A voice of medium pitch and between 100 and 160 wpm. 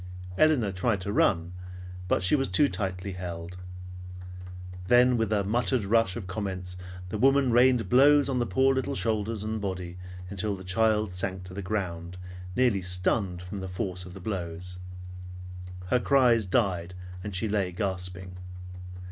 No: low, 100 Hz; average, 155 wpm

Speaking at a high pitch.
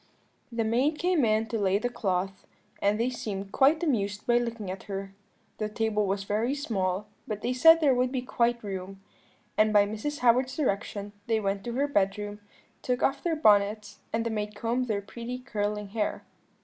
Yes: high, 220 Hz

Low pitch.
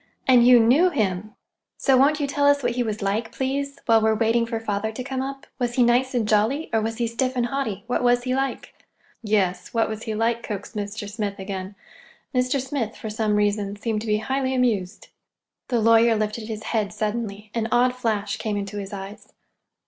No: high, 225 Hz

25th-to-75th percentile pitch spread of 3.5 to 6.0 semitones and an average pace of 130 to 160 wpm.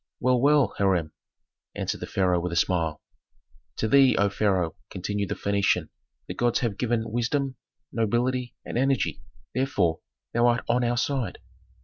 Yes: average, 4.6 semitones; average, 150 wpm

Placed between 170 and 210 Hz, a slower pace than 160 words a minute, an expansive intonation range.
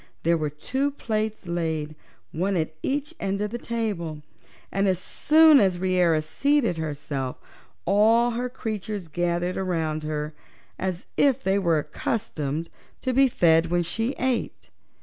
Yes: medium, 185 Hz; average, 145 wpm; wide, 6.1 semitones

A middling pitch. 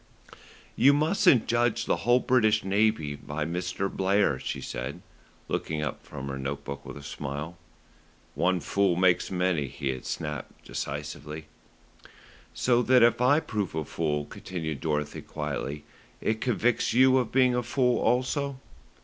No: very low, 95 Hz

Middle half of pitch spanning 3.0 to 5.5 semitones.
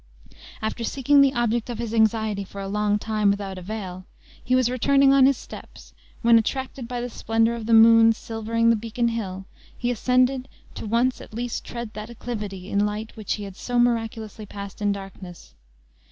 No: narrow, 2.6 semitones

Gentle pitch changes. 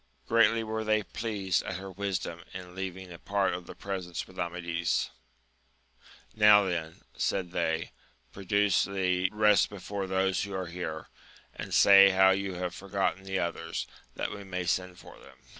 Yes: narrow, 1.9 semitones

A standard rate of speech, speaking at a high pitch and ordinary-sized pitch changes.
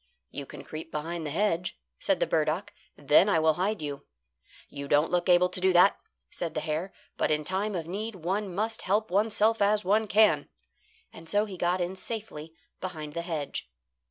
No: average, 190 wpm; medium, 180 Hz; average, 4.5 semitones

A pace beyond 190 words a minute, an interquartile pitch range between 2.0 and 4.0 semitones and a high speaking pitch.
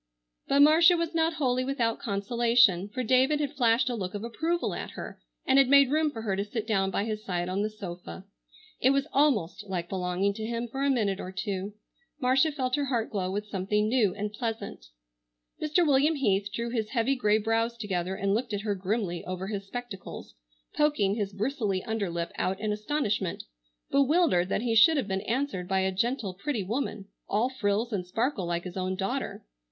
No: average, 200 wpm; average, 5.1 semitones; high, 220 Hz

